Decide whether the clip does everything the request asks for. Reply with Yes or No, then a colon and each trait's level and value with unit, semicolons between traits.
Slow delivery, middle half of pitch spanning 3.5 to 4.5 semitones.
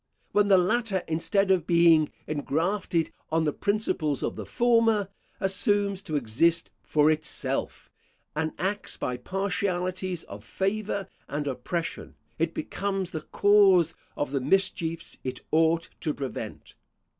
Yes: slow, 130 wpm; average, 4.2 semitones